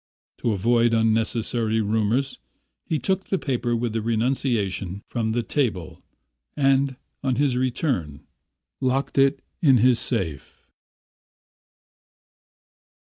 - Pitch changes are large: No, average, 3.4 semitones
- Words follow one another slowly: Yes, slow, 105 wpm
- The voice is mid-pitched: No, low, 120 Hz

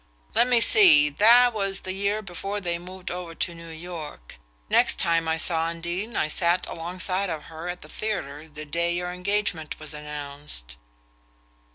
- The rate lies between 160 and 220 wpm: Yes, average, 170 wpm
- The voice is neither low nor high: Yes, medium, 170 Hz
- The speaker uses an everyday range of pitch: Yes, average, 3.3 semitones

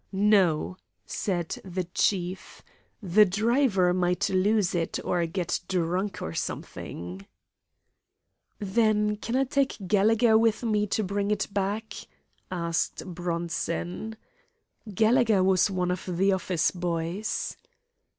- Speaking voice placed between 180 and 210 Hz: Yes, high, 190 Hz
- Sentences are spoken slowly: Yes, slow, 110 wpm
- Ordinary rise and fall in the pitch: Yes, average, 3.1 semitones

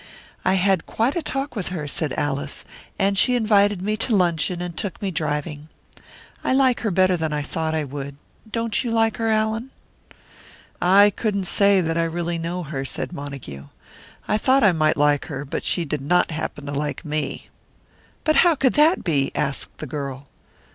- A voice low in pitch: No, medium, 175 Hz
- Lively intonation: Yes, wide, 6.2 semitones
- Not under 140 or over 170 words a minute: No, average, 190 wpm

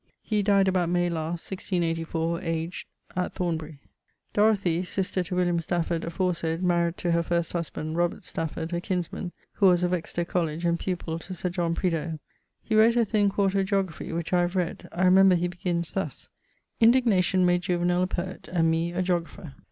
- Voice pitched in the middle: Yes, medium, 175 Hz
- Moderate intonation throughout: No, narrow, 1.8 semitones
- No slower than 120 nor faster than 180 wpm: Yes, average, 175 wpm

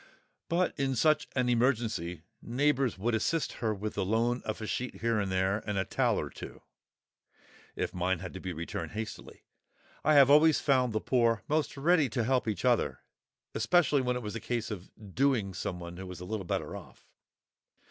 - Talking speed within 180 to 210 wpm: Yes, average, 190 wpm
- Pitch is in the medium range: No, low, 115 Hz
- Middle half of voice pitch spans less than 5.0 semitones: No, wide, 5.4 semitones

